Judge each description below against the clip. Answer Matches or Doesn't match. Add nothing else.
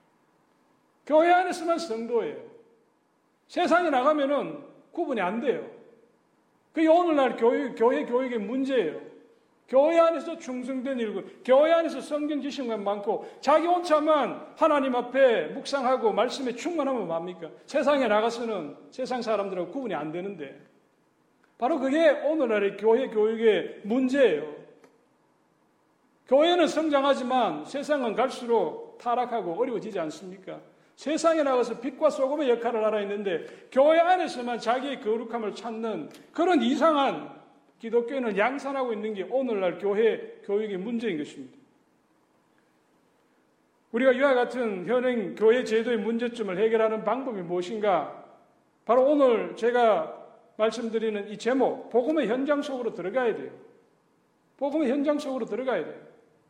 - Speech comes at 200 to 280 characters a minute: Doesn't match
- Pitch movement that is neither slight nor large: Matches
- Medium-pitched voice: Doesn't match